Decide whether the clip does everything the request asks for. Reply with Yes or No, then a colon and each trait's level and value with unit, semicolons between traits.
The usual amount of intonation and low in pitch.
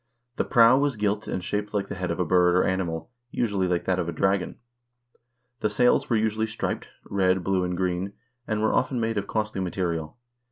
Yes: average, 3.1 semitones; very low, 95 Hz